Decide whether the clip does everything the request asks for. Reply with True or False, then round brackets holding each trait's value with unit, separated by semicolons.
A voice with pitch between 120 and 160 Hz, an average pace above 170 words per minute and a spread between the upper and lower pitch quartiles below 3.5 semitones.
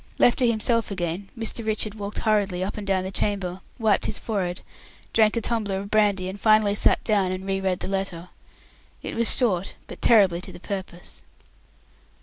False (200 Hz; 185 wpm; 2.5 semitones)